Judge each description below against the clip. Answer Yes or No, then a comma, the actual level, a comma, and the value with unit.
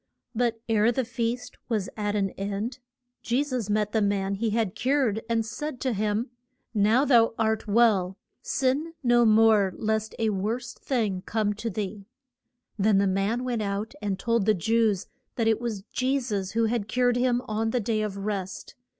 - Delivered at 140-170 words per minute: No, average, 180 wpm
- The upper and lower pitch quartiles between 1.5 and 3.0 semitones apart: Yes, average, 2.7 semitones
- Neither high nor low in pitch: No, high, 220 Hz